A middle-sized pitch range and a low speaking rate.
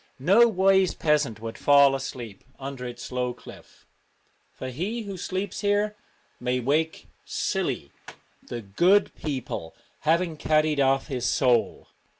No: wide, 6.6 semitones; slow, 130 wpm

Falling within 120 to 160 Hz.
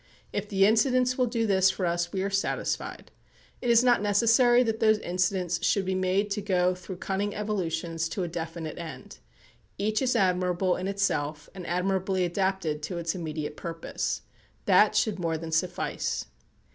No: high, 190 Hz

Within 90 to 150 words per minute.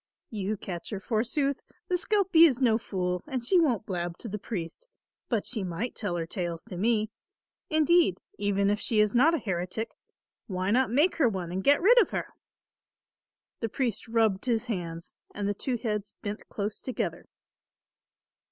No: average, 175 wpm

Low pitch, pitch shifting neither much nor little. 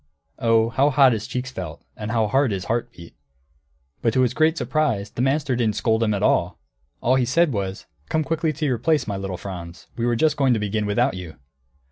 Yes: low, 120 Hz; average, 4.6 semitones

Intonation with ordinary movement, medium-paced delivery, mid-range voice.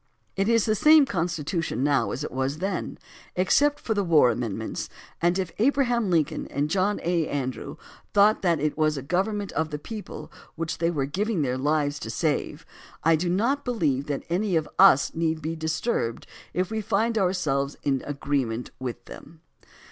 No: wide, 5.7 semitones; average, 180 wpm; medium, 165 Hz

